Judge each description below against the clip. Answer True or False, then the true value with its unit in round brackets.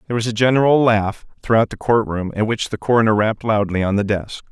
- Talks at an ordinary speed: False (225 wpm)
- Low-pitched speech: True (110 Hz)